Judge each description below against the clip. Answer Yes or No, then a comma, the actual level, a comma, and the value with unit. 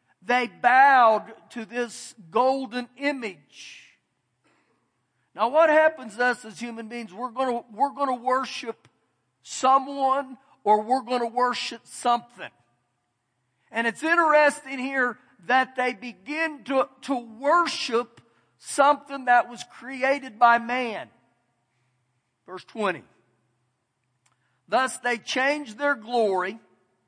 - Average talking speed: No, slow, 115 wpm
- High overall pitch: Yes, high, 245 Hz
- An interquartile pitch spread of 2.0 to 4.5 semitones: No, average, 5.2 semitones